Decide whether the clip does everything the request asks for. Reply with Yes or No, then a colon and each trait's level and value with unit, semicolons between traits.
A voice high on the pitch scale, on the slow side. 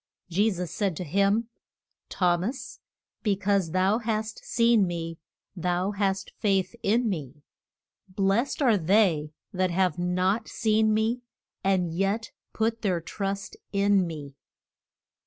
Yes: high, 195 Hz; slow, 130 wpm